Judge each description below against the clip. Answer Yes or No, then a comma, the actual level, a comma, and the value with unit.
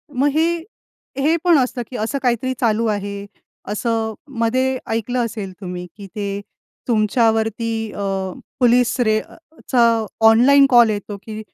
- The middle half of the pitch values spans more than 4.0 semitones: No, average, 3.0 semitones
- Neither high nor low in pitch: No, high, 230 Hz